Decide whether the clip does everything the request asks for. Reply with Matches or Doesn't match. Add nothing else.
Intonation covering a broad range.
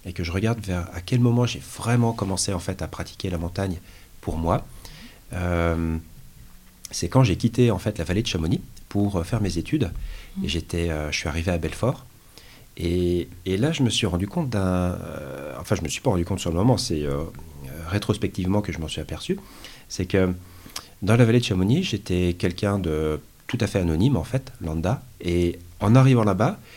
Doesn't match